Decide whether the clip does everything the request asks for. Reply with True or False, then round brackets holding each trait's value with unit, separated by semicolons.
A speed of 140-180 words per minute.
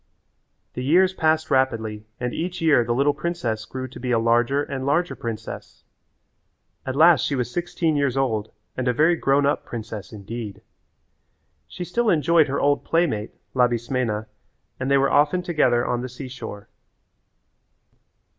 True (155 wpm)